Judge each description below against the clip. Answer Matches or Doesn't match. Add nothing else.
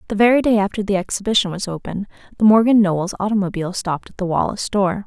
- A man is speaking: Doesn't match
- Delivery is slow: Doesn't match